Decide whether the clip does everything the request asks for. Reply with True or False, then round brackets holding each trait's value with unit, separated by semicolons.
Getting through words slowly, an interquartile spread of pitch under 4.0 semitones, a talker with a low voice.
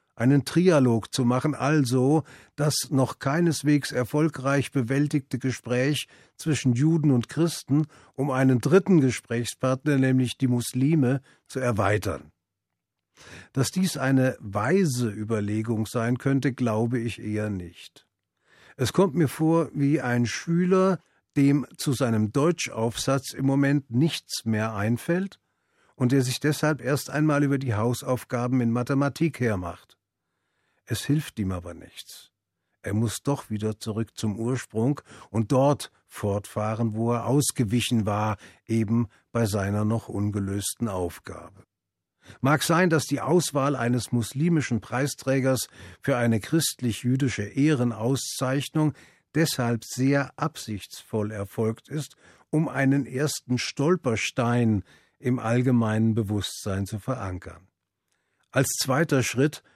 False (120 wpm; 4.5 semitones; 125 Hz)